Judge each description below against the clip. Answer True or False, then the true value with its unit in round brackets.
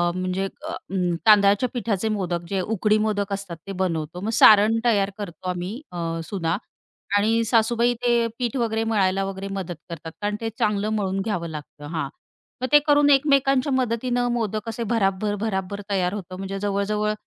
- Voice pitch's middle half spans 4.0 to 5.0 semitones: False (3.1 semitones)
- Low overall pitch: False (205 Hz)